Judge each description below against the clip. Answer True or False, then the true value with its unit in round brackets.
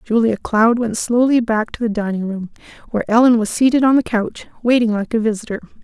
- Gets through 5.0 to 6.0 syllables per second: True (5.9 syllables/s)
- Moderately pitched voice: False (225 Hz)